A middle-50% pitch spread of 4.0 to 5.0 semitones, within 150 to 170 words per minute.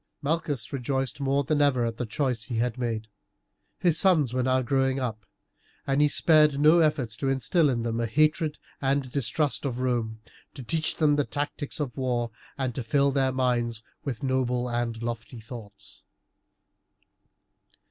No: average, 3.3 semitones; average, 165 wpm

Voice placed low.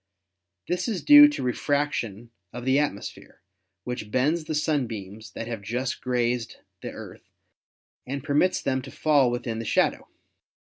Yes: low, 125 Hz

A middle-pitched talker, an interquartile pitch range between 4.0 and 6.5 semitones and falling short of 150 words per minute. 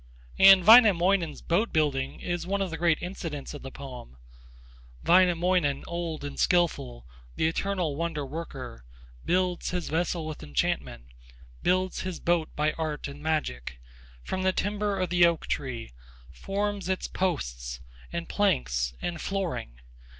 Yes: medium, 170 Hz; average, 4.8 semitones; average, 140 wpm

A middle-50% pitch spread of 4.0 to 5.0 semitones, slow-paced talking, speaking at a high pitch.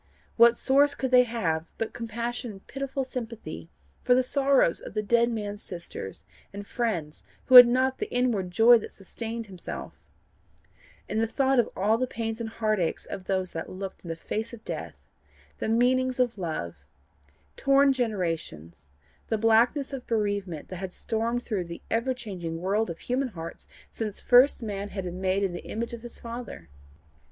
No: average, 4.6 semitones; average, 175 wpm; high, 225 Hz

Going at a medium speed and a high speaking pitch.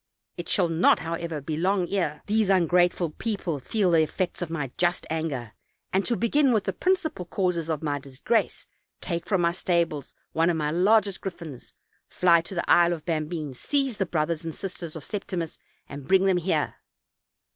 No: average, 180 wpm; medium, 170 Hz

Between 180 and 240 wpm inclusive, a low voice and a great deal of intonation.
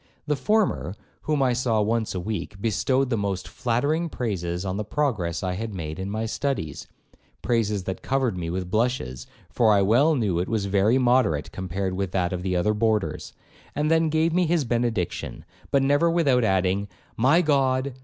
Yes: average, 185 wpm; low, 110 Hz; wide, 6.1 semitones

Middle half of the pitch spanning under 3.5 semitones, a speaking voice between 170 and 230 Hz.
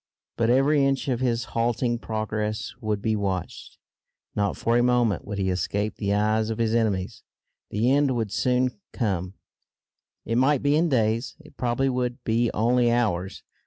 No: average, 2.8 semitones; low, 115 Hz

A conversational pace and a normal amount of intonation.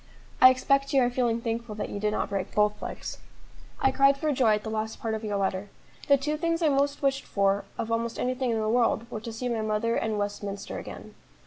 No: fast, 235 wpm; average, 3.9 semitones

